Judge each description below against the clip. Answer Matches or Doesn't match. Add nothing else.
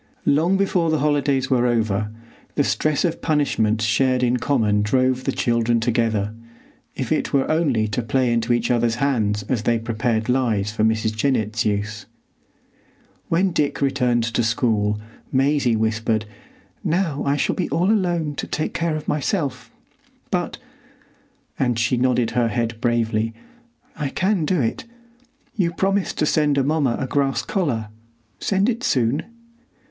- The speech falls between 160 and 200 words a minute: Doesn't match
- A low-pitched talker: Matches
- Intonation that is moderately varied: Matches